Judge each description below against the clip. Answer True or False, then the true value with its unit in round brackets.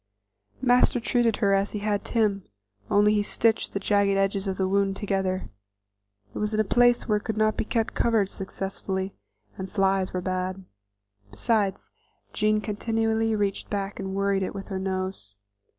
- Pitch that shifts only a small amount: True (2.1 semitones)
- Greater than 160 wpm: True (170 wpm)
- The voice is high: True (200 Hz)